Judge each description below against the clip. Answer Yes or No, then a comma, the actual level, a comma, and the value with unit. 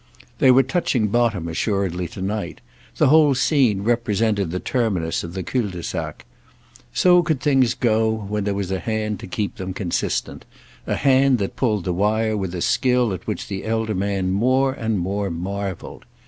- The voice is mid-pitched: No, low, 105 Hz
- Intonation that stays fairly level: No, average, 4.2 semitones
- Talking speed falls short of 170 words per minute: No, average, 175 wpm